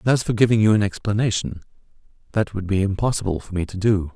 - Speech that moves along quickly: Yes, fast, 215 wpm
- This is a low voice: Yes, low, 100 Hz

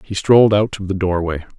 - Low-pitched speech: Yes, low, 100 Hz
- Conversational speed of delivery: No, fast, 225 wpm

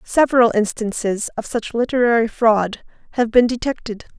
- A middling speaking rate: No, slow, 130 wpm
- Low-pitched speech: No, high, 230 Hz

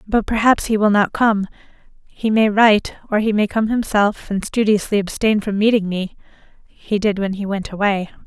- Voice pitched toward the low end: No, high, 210 Hz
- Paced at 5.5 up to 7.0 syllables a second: No, 5.1 syllables/s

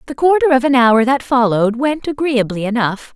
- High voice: Yes, very high, 250 Hz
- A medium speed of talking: Yes, average, 190 wpm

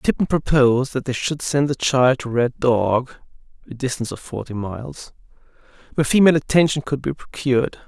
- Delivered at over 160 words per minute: No, average, 150 wpm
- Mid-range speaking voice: No, low, 130 Hz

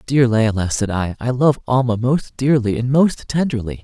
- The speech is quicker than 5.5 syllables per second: No, 4.8 syllables/s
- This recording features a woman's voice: No, male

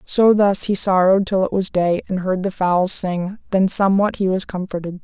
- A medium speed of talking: No, fast, 215 wpm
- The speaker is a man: No, female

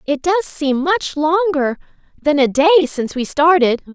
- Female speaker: Yes, female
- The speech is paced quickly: No, average, 165 wpm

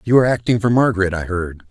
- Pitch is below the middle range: Yes, low, 105 Hz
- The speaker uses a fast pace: Yes, fast, 245 wpm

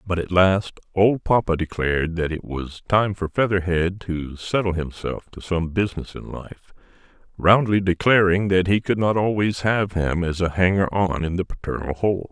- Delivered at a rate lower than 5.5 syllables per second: Yes, 4.7 syllables/s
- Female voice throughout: No, male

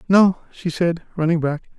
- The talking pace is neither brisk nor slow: Yes, average, 170 wpm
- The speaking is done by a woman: No, male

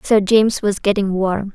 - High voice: Yes, high, 200 Hz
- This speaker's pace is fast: No, average, 195 wpm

